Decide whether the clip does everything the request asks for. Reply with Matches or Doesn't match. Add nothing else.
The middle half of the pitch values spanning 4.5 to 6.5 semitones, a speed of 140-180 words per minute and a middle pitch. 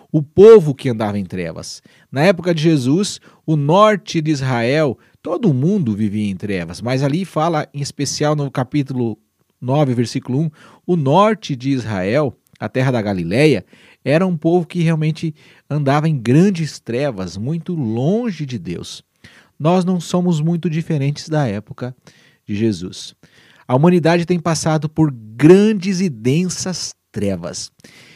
Matches